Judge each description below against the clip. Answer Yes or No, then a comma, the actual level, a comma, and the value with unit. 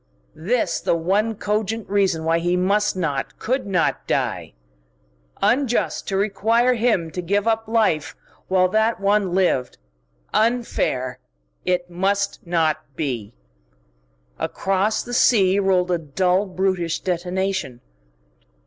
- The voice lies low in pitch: No, high, 190 Hz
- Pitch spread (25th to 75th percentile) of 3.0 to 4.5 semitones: Yes, average, 3.6 semitones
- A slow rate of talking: Yes, slow, 120 wpm